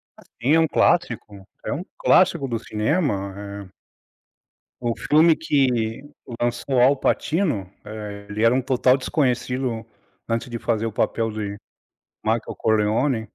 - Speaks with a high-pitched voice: No, low, 115 Hz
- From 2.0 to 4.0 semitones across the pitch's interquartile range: Yes, average, 3.7 semitones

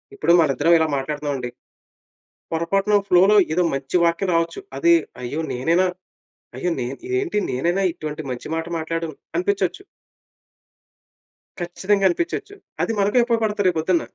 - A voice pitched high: No, medium, 170 Hz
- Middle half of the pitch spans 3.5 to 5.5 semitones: Yes, average, 4.1 semitones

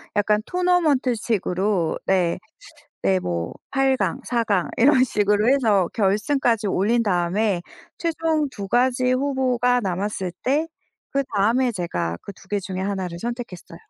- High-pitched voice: Yes, high, 215 Hz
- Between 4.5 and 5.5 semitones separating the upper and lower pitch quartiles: Yes, average, 5.2 semitones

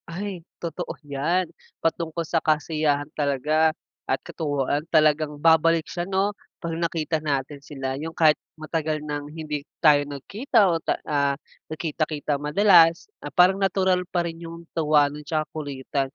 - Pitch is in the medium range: Yes, medium, 155 Hz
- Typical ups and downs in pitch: No, narrow, 2.3 semitones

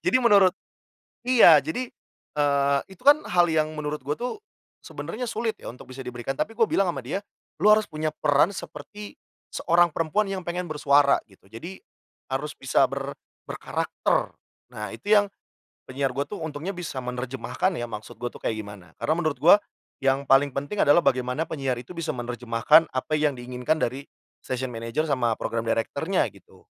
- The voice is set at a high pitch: No, medium, 145 Hz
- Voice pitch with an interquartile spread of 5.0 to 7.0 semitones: Yes, wide, 5.6 semitones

